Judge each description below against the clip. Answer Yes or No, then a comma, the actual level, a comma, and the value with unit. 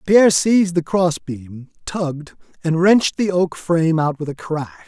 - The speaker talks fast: No, average, 170 wpm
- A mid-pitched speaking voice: Yes, medium, 165 Hz